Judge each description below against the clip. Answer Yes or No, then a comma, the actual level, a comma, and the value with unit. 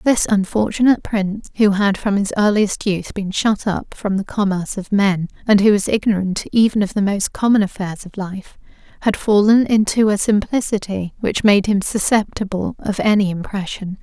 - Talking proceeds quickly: No, average, 175 wpm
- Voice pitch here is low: No, high, 200 Hz